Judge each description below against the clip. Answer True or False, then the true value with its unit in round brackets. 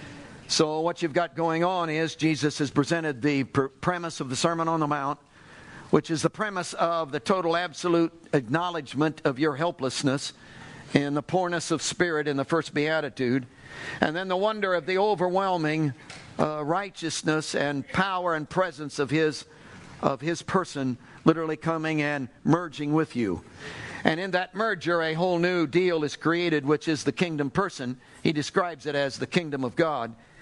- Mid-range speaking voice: True (160 Hz)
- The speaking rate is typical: True (170 wpm)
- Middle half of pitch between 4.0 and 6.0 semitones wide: False (3.1 semitones)